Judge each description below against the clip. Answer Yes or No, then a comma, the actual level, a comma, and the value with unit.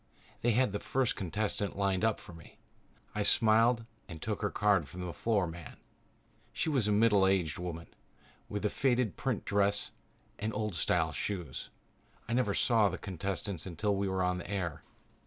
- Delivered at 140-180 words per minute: Yes, average, 175 wpm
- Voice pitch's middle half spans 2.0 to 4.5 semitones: Yes, average, 3.2 semitones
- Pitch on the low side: Yes, low, 100 Hz